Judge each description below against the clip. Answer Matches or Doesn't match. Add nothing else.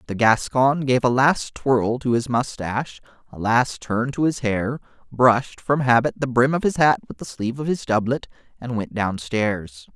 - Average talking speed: Matches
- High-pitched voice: Doesn't match